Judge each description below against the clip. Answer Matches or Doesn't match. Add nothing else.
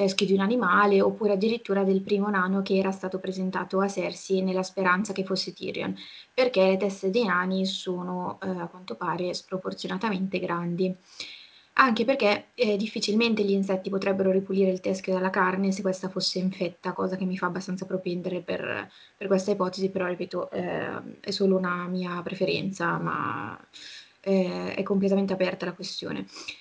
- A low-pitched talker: Doesn't match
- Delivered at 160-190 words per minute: Matches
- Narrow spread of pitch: Matches